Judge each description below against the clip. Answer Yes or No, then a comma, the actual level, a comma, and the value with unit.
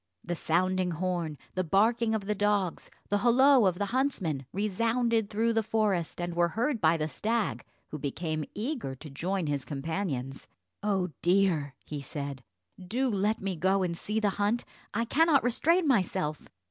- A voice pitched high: Yes, high, 195 Hz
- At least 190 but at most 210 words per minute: No, average, 165 wpm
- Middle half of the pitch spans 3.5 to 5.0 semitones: No, wide, 5.4 semitones